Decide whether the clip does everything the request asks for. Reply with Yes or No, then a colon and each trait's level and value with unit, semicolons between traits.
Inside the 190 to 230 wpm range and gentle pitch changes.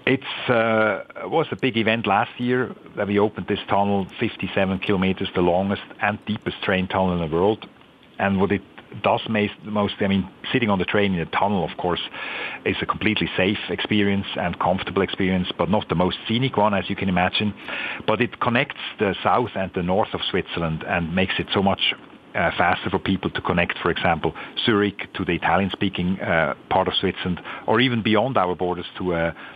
Yes: average, 200 wpm; narrow, 2.3 semitones